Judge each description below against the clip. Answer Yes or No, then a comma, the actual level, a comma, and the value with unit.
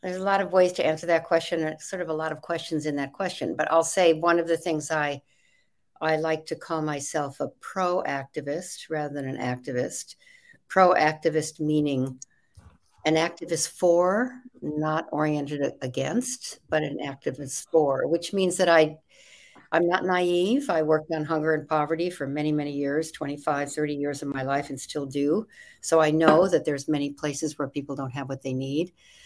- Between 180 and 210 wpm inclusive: Yes, average, 185 wpm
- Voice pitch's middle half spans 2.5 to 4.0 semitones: Yes, average, 2.8 semitones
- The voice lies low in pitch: No, medium, 155 Hz